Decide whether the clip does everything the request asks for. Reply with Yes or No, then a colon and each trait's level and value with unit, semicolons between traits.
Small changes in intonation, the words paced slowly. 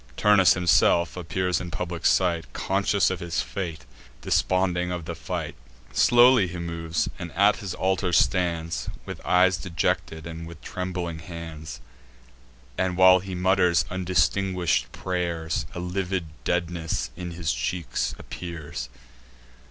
Yes: narrow, 1.8 semitones; slow, 125 wpm